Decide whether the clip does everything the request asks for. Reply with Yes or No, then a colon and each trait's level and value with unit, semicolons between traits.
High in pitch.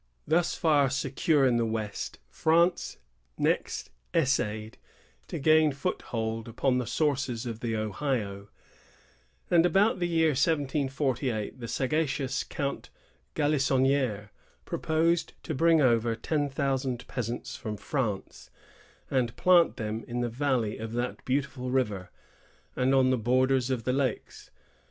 No: low, 130 Hz